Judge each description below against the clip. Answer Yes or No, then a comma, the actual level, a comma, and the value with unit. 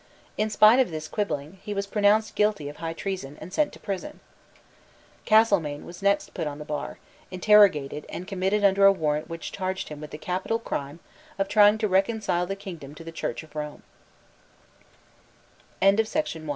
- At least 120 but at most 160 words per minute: No, average, 175 wpm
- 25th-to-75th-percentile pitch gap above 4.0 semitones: Yes, average, 5.0 semitones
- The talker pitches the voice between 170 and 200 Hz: Yes, high, 190 Hz